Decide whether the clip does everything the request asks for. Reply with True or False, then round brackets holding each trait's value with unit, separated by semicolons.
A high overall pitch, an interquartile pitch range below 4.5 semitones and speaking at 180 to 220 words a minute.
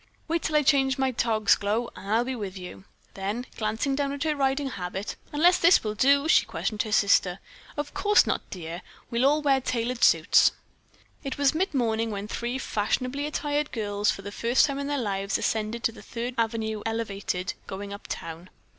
False (235 Hz; 5.3 semitones; 190 wpm)